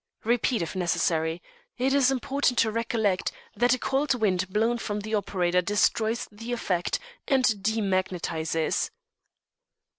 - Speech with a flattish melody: No, average, 4.8 semitones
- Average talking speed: No, slow, 125 wpm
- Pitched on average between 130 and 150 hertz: No, high, 215 Hz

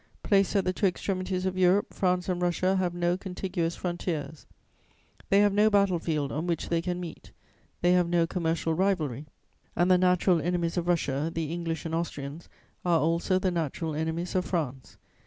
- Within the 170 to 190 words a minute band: Yes, average, 180 wpm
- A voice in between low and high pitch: Yes, medium, 175 Hz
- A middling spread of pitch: No, narrow, 2.0 semitones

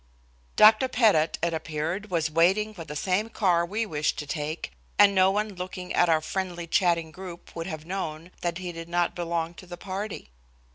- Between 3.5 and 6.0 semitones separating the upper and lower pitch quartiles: No, average, 2.8 semitones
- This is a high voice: No, medium, 175 Hz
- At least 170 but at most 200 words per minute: Yes, average, 190 wpm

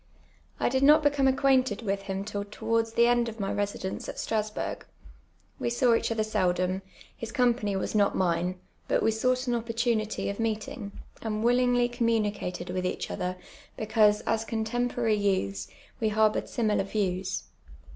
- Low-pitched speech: No, high, 220 Hz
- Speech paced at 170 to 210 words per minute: No, average, 155 wpm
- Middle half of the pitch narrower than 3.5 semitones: Yes, average, 2.9 semitones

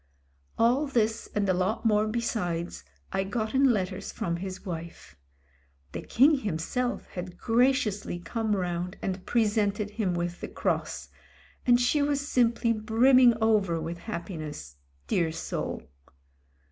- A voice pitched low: No, high, 210 Hz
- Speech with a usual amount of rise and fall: Yes, average, 4.8 semitones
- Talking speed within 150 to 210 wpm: No, slow, 135 wpm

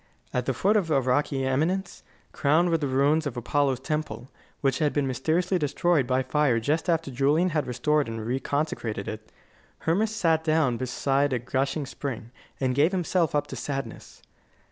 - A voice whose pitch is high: No, medium, 145 Hz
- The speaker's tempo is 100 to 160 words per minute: No, average, 170 wpm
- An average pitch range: Yes, average, 3.7 semitones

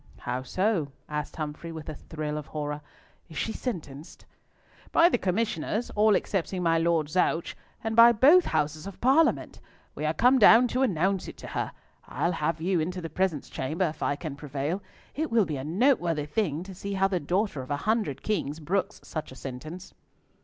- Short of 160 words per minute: No, average, 190 wpm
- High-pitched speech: No, medium, 170 Hz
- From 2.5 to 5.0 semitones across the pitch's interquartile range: No, wide, 5.4 semitones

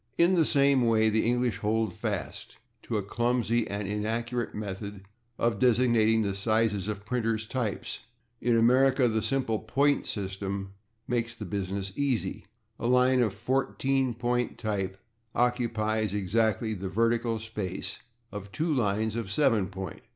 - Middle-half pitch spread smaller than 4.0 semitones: Yes, average, 3.0 semitones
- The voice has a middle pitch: No, low, 110 Hz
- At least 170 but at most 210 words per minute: No, average, 145 wpm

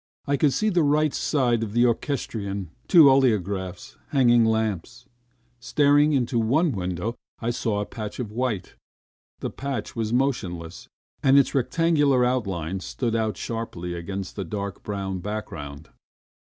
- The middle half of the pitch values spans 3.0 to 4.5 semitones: No, wide, 5.5 semitones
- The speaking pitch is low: Yes, low, 115 Hz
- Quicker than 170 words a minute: No, average, 140 wpm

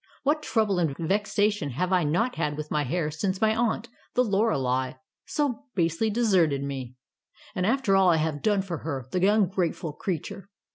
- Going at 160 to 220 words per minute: Yes, average, 175 wpm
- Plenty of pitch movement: Yes, wide, 5.9 semitones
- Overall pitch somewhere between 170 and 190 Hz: Yes, medium, 185 Hz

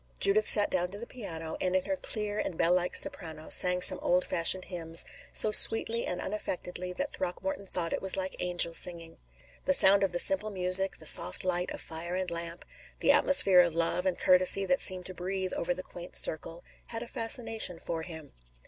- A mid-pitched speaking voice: Yes, medium, 180 Hz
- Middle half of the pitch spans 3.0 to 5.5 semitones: No, narrow, 2.4 semitones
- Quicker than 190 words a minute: Yes, average, 200 wpm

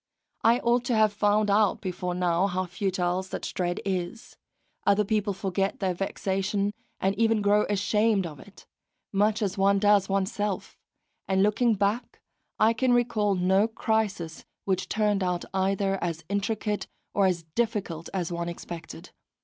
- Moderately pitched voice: No, high, 200 Hz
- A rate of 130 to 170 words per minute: Yes, average, 150 wpm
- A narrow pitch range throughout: Yes, narrow, 2.3 semitones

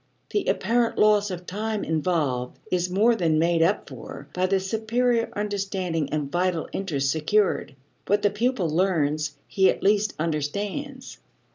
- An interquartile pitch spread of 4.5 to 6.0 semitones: Yes, average, 4.9 semitones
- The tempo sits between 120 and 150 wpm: Yes, average, 145 wpm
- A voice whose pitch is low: No, medium, 185 Hz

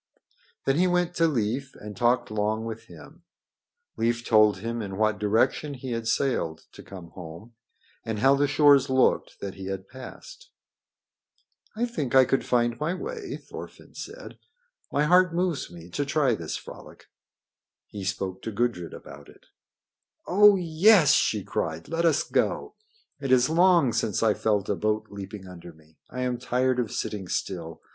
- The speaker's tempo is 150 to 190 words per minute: Yes, average, 165 wpm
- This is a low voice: Yes, low, 120 Hz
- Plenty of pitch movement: Yes, wide, 6.3 semitones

